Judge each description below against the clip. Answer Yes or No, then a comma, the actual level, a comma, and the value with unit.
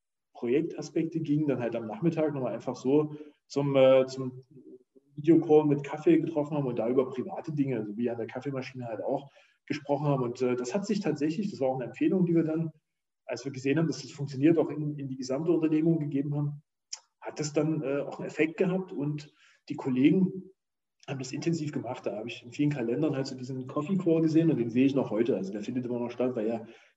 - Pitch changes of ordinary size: Yes, average, 3.4 semitones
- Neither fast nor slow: No, fast, 225 wpm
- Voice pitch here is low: No, medium, 145 Hz